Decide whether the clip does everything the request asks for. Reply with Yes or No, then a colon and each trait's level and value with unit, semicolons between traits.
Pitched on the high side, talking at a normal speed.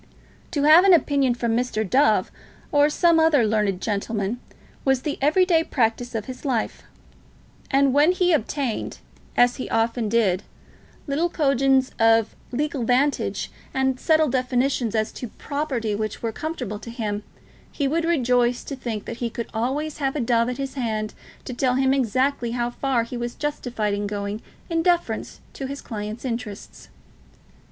Yes: very high, 250 Hz; average, 165 wpm